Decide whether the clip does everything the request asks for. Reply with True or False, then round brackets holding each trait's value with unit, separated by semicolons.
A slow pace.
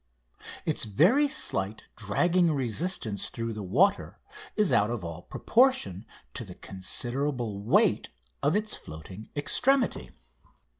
True (115 wpm)